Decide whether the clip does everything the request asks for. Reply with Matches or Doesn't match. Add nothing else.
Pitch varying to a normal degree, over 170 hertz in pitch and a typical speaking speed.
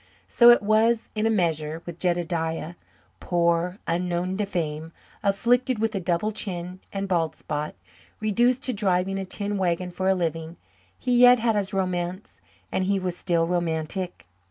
Matches